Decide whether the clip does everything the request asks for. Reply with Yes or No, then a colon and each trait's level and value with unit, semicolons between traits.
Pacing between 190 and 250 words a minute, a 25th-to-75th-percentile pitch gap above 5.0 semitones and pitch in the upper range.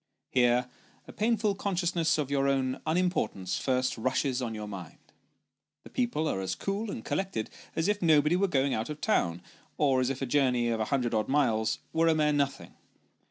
No: average, 195 wpm; wide, 5.6 semitones; medium, 140 Hz